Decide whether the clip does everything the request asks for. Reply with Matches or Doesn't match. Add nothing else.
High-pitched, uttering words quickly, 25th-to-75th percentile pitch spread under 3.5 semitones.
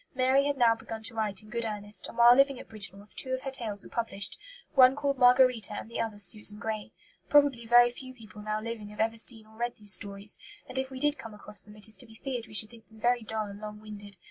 Matches